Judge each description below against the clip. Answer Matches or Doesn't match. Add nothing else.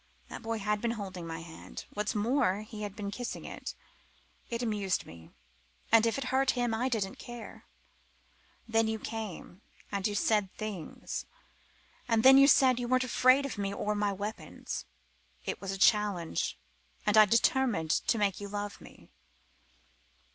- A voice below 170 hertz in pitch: Doesn't match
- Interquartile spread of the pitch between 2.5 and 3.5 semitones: Matches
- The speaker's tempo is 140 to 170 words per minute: Matches